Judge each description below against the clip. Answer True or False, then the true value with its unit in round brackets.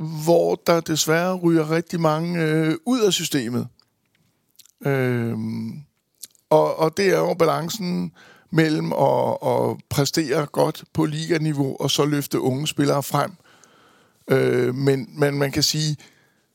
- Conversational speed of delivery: False (130 wpm)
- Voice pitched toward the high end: False (155 Hz)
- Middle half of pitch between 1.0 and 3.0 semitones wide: True (2.7 semitones)